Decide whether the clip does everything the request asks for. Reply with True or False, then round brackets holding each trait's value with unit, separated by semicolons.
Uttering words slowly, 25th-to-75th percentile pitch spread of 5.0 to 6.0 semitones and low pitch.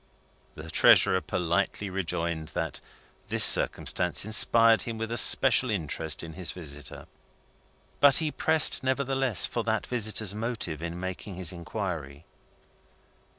True (125 wpm; 5.5 semitones; 95 Hz)